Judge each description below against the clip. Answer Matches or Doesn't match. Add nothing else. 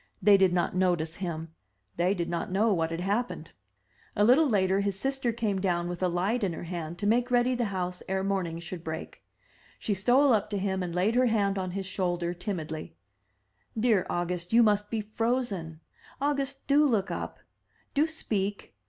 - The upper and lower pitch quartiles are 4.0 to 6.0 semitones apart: Matches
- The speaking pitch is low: Doesn't match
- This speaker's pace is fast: Doesn't match